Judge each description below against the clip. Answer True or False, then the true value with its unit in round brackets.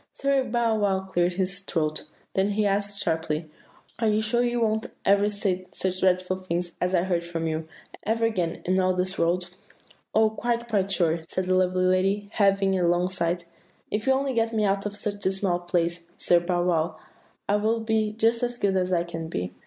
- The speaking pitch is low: False (190 Hz)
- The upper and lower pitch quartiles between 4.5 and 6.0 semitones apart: False (3.4 semitones)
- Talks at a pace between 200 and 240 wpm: True (205 wpm)